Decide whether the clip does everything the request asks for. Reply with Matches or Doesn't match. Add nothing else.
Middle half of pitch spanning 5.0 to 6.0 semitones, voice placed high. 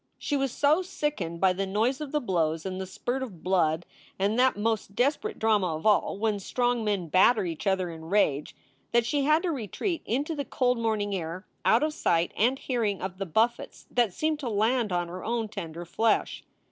Matches